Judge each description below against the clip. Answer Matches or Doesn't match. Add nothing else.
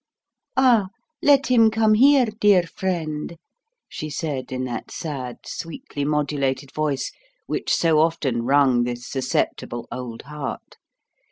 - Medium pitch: Matches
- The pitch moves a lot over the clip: Matches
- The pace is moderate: Doesn't match